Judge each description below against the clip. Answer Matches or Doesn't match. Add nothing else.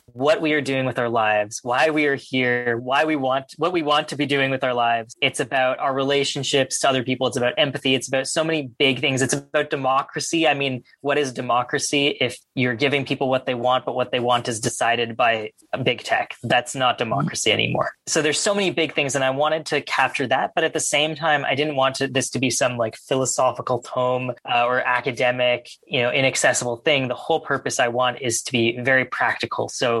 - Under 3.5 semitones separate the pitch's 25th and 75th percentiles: Matches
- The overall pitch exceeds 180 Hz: Doesn't match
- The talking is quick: Matches